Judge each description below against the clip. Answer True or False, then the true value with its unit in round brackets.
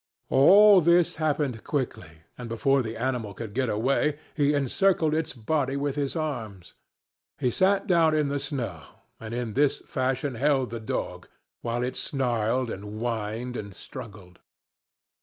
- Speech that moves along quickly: False (150 wpm)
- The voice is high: False (130 Hz)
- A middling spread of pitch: True (4.5 semitones)